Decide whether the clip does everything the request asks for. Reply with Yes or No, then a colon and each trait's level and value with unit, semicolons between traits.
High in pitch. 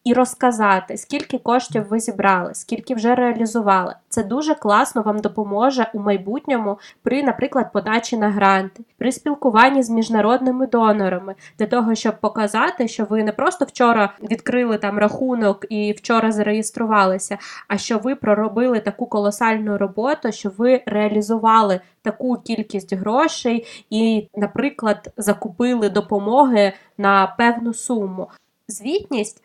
Yes: high, 225 Hz